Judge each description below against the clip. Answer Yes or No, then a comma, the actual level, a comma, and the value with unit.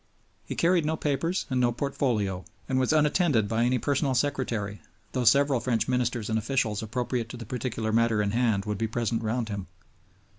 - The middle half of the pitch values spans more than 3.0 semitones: Yes, average, 3.4 semitones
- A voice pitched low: Yes, low, 120 Hz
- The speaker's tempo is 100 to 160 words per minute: No, average, 185 wpm